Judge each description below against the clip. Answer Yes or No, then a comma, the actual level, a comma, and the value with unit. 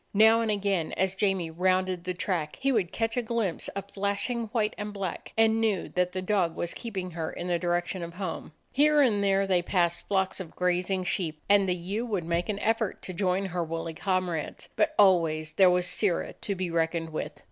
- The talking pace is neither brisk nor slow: No, fast, 210 wpm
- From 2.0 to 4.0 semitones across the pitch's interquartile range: Yes, average, 2.9 semitones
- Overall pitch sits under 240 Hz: Yes, medium, 185 Hz